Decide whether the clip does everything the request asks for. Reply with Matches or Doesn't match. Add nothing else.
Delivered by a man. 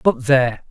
Matches